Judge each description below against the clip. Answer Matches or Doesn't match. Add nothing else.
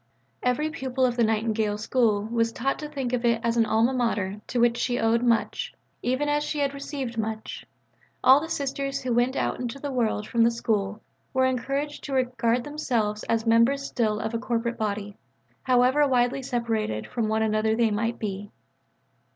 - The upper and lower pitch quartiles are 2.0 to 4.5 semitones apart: Matches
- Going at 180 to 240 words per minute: Matches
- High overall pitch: Matches